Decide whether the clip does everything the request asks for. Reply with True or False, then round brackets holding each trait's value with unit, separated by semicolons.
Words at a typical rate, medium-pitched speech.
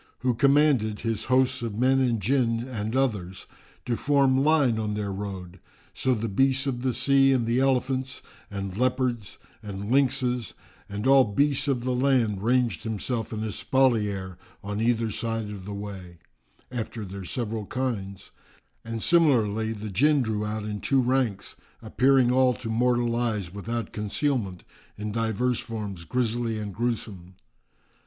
False (150 wpm; 115 Hz)